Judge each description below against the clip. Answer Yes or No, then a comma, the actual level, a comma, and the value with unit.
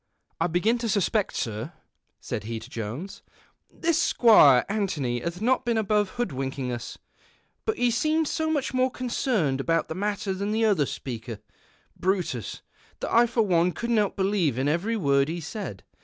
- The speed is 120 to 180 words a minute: Yes, average, 170 wpm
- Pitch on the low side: No, high, 190 Hz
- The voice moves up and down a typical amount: No, wide, 8.7 semitones